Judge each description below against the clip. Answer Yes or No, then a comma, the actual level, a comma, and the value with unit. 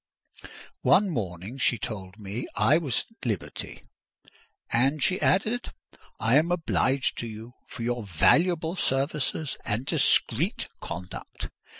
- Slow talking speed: Yes, slow, 120 wpm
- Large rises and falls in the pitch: Yes, wide, 6.6 semitones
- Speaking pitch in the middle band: No, low, 125 Hz